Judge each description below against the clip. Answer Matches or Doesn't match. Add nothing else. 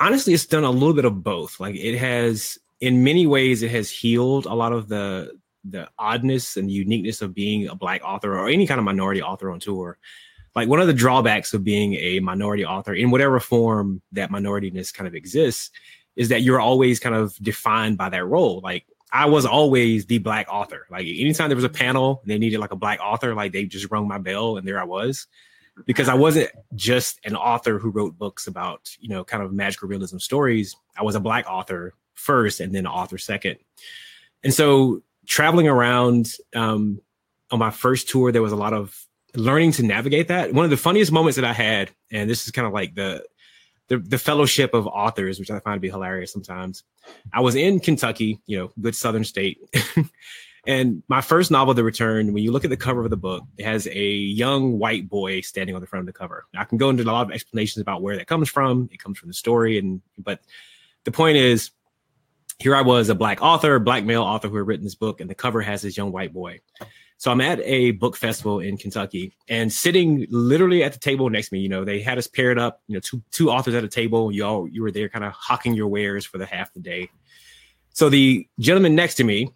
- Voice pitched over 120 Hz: Doesn't match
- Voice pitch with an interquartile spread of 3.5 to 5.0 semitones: Matches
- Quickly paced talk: Matches